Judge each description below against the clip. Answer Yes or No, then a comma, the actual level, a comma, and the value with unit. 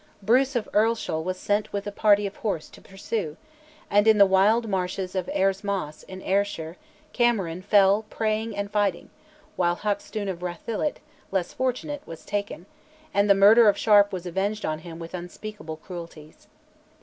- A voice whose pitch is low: No, high, 200 Hz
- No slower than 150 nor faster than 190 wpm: Yes, average, 165 wpm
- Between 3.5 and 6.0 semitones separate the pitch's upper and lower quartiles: No, average, 2.8 semitones